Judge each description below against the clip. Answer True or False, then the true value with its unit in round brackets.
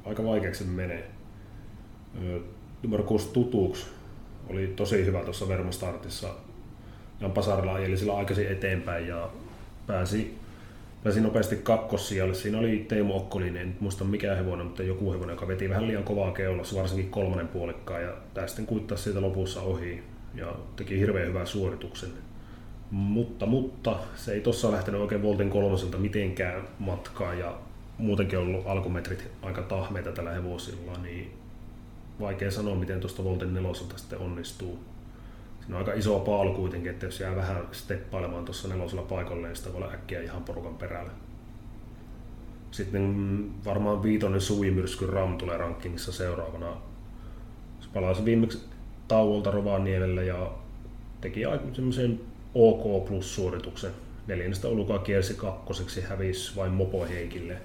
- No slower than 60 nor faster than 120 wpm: False (135 wpm)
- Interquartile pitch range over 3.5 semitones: False (2.9 semitones)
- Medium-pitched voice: False (100 Hz)